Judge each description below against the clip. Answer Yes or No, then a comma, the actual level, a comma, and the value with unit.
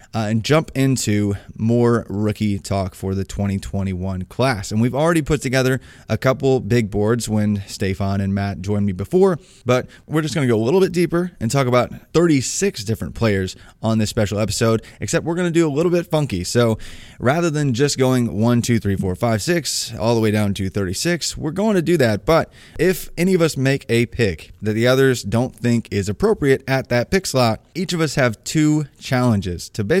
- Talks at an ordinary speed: No, fast, 210 wpm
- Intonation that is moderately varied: No, wide, 6.0 semitones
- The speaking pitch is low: Yes, low, 120 Hz